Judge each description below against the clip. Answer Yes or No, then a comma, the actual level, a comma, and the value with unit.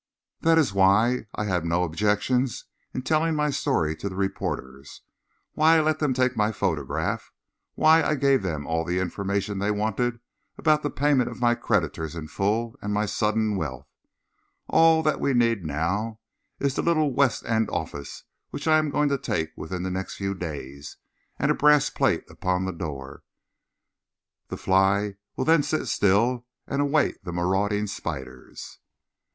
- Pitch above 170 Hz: No, low, 105 Hz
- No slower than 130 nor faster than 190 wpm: Yes, average, 170 wpm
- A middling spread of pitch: No, wide, 7.3 semitones